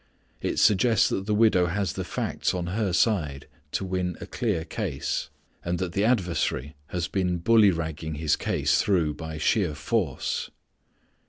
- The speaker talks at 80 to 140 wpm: No, average, 160 wpm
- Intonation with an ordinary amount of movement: Yes, average, 4.2 semitones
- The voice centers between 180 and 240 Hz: No, very low, 90 Hz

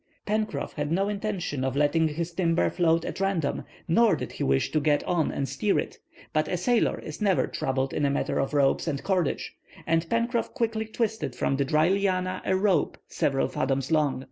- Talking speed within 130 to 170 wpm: No, average, 195 wpm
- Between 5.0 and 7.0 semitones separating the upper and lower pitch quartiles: Yes, wide, 5.4 semitones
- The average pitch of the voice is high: No, medium, 165 Hz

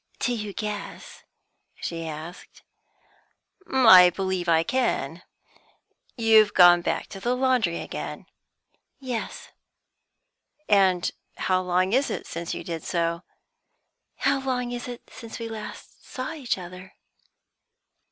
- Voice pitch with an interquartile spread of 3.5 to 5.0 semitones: No, wide, 5.5 semitones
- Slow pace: Yes, slow, 125 wpm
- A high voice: Yes, high, 200 Hz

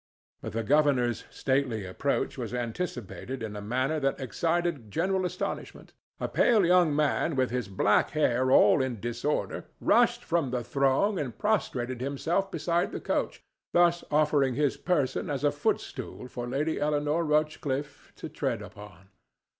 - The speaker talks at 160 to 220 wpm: No, average, 150 wpm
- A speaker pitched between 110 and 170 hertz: Yes, medium, 140 Hz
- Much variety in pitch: No, average, 4.8 semitones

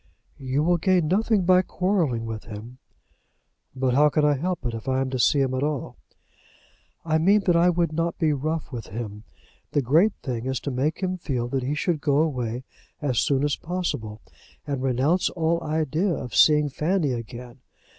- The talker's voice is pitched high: No, medium, 145 Hz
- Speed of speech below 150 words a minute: No, average, 190 wpm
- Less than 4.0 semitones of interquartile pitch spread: No, average, 4.8 semitones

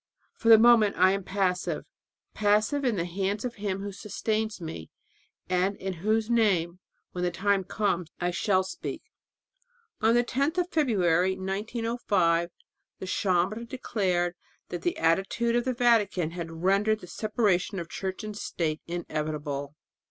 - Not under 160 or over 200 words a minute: No, average, 150 wpm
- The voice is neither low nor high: No, high, 195 Hz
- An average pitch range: Yes, average, 3.8 semitones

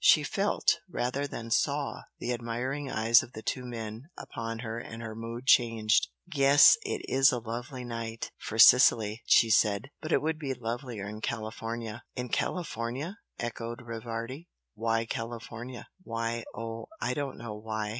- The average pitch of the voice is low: Yes, low, 115 Hz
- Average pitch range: No, narrow, 2.1 semitones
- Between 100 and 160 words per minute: Yes, average, 155 wpm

